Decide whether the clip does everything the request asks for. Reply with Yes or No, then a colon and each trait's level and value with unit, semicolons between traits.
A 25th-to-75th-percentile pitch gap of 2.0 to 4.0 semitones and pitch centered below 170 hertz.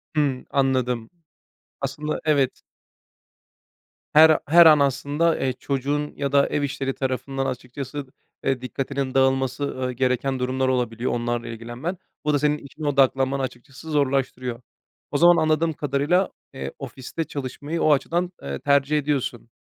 Yes: narrow, 2.4 semitones; low, 135 Hz